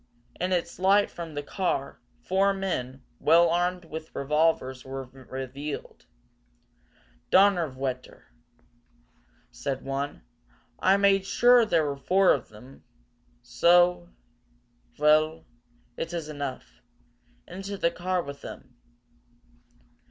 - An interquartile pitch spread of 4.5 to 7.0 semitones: Yes, average, 5.1 semitones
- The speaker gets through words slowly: Yes, slow, 105 wpm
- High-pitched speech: No, medium, 160 Hz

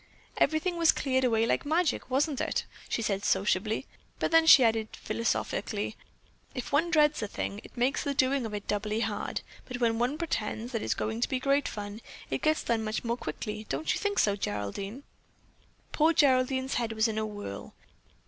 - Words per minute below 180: No, average, 190 wpm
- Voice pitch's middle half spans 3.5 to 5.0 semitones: Yes, average, 4.7 semitones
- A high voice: Yes, high, 235 Hz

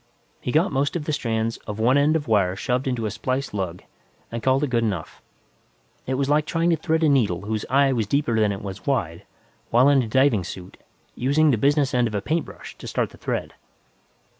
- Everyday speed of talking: No, fast, 220 wpm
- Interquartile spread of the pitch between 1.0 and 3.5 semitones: No, average, 4.9 semitones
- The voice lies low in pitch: Yes, low, 125 Hz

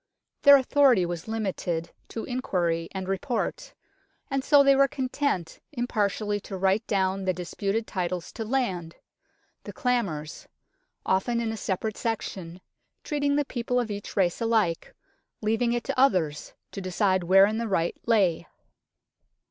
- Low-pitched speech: No, high, 205 Hz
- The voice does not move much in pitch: No, average, 4.8 semitones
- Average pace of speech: Yes, average, 145 wpm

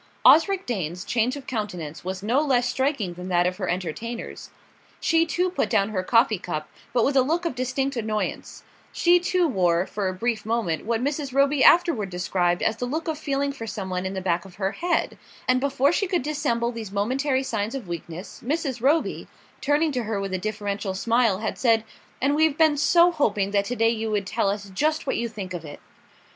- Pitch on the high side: Yes, high, 230 Hz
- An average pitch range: No, wide, 6.4 semitones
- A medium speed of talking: No, fast, 210 wpm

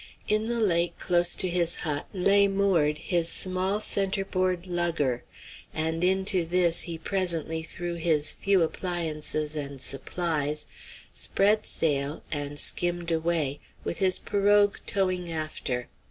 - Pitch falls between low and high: Yes, medium, 175 Hz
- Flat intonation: No, average, 3.3 semitones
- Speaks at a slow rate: Yes, slow, 125 wpm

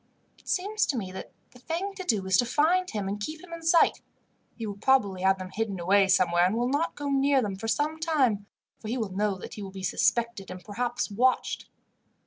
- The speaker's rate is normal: No, fast, 230 wpm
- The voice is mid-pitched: No, high, 225 Hz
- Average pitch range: No, wide, 7.0 semitones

